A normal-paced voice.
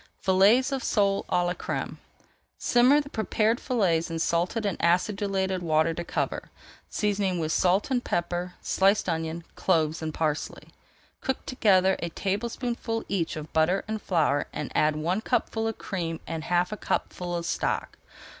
Yes: average, 155 wpm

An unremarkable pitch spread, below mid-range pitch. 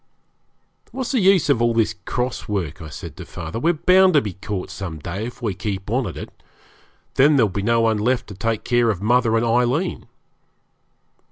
Yes: average, 3.9 semitones; low, 115 Hz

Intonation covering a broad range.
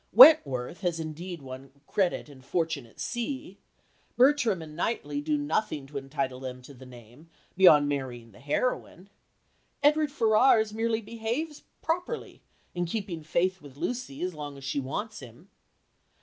Yes: wide, 8.8 semitones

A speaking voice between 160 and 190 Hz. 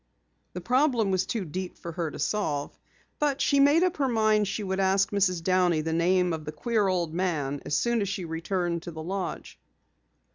Yes: medium, 185 Hz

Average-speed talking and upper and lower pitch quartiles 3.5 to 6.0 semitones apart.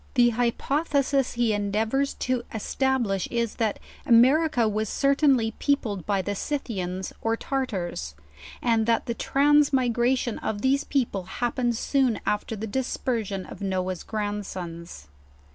No: slow, 125 wpm; average, 4.4 semitones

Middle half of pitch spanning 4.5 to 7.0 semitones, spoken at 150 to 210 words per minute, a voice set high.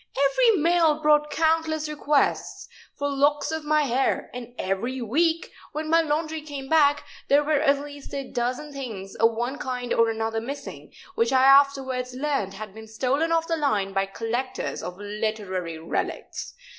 Yes: average, 4.8 semitones; average, 165 wpm; very high, 275 Hz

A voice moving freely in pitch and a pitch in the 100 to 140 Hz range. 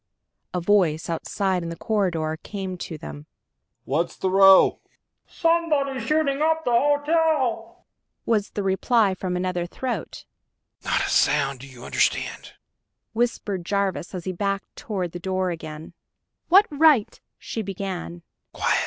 No: wide, 5.8 semitones; high, 195 Hz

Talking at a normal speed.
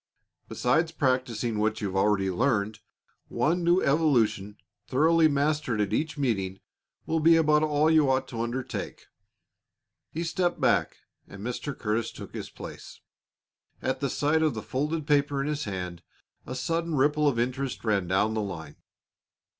Yes: average, 155 wpm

